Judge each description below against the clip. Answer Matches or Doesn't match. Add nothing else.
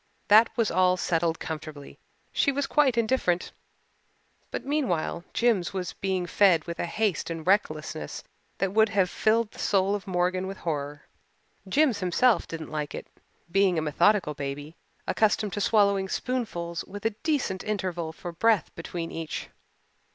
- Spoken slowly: Doesn't match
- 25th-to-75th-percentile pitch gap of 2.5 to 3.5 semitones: Doesn't match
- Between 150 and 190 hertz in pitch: Matches